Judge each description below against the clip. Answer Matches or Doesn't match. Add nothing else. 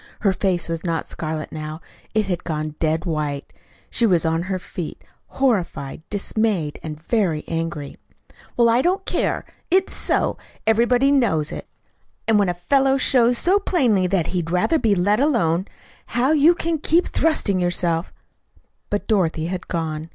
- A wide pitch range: Matches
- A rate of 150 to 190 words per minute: Matches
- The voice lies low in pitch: Doesn't match